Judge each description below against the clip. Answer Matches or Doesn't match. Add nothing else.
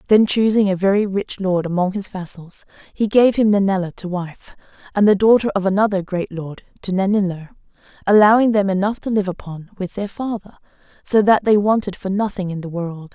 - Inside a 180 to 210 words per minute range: Matches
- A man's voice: Doesn't match